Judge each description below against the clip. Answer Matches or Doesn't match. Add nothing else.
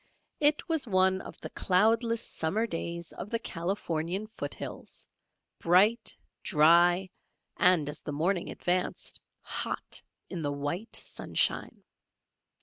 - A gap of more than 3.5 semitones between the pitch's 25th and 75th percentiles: Matches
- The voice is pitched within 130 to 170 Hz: Doesn't match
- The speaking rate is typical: Doesn't match